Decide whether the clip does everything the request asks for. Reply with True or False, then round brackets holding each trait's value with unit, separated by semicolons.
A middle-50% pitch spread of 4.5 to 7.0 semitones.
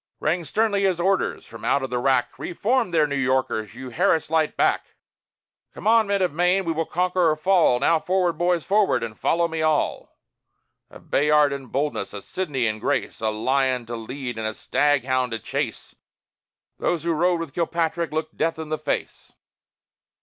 True (5.2 semitones)